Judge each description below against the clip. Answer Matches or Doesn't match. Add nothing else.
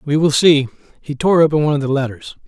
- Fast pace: Matches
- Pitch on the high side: Doesn't match